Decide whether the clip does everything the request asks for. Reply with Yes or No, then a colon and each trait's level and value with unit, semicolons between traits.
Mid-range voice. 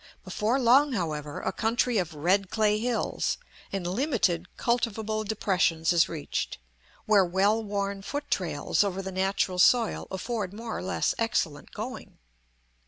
No: high, 200 Hz